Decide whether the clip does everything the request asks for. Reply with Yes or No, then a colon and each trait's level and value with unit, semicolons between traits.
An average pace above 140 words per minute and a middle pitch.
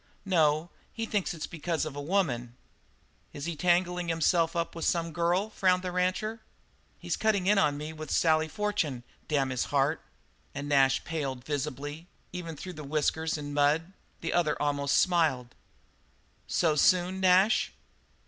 Yes: average, 150 wpm; medium, 160 Hz